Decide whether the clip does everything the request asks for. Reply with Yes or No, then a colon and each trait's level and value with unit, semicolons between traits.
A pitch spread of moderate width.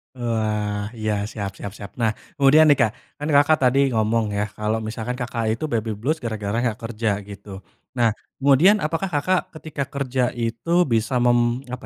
Yes: average, 4.2 semitones